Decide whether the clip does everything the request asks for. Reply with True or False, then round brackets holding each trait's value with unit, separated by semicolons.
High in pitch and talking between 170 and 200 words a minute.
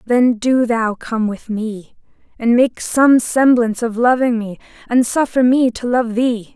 True (235 Hz; 175 wpm)